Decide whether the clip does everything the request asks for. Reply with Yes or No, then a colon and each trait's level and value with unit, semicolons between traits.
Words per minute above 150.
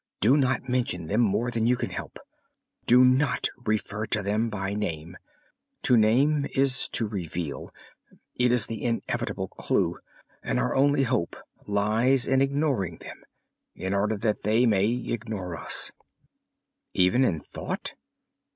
No: average, 140 wpm